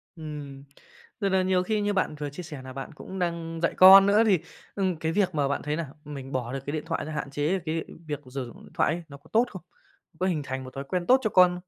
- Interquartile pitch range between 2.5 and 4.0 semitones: No, average, 4.7 semitones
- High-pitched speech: No, medium, 160 Hz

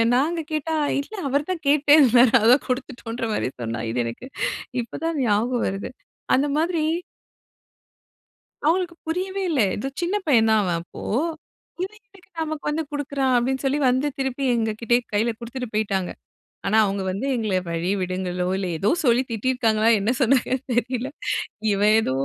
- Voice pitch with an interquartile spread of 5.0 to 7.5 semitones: Yes, average, 5.3 semitones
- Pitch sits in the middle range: No, very high, 250 Hz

